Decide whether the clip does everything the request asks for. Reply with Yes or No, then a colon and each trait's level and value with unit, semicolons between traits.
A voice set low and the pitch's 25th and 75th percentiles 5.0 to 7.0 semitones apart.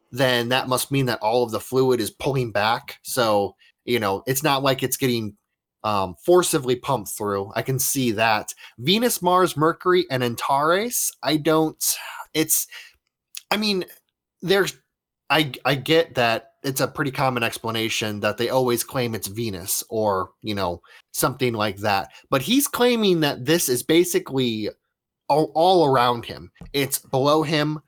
Yes: low, 130 Hz; wide, 5.6 semitones